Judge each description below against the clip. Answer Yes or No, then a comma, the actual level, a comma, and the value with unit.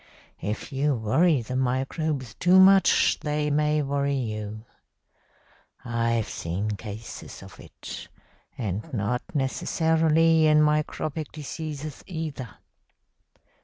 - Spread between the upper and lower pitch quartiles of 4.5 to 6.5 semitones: Yes, average, 5.0 semitones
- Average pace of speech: No, slow, 100 wpm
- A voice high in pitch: No, medium, 140 Hz